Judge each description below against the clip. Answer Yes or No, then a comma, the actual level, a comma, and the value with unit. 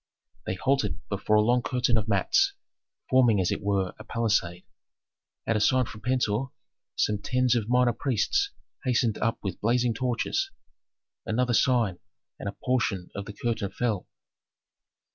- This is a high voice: No, low, 115 Hz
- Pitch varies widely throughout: No, average, 3.5 semitones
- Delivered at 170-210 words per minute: No, average, 150 wpm